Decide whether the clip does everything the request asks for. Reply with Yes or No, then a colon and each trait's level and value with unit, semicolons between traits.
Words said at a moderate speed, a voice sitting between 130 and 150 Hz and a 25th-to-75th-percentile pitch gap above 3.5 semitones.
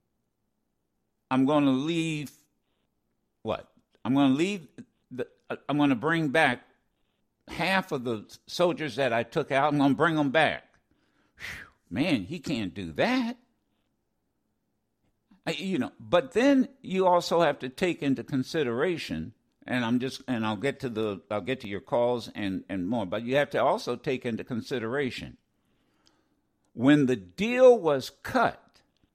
Yes: average, 155 wpm; medium, 140 Hz; wide, 5.6 semitones